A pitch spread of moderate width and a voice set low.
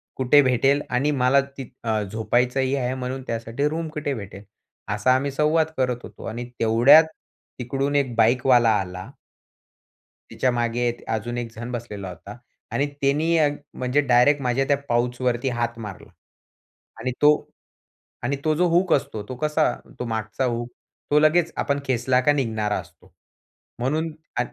Yes: average, 3.2 semitones; low, 125 Hz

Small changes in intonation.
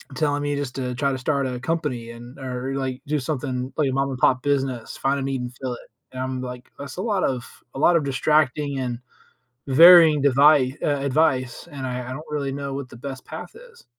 Yes: narrow, 2.2 semitones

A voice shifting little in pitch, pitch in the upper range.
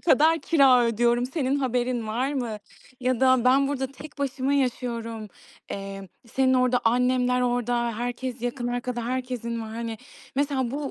Yes: narrow, 1.9 semitones; very high, 250 Hz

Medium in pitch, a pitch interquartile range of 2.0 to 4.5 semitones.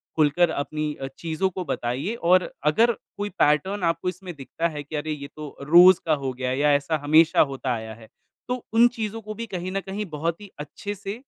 No: medium, 165 Hz; average, 4.9 semitones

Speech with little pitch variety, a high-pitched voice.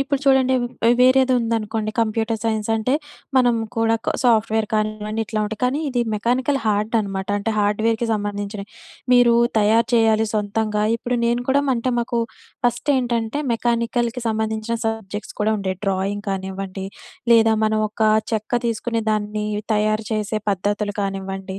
Yes: narrow, 2.1 semitones; high, 220 Hz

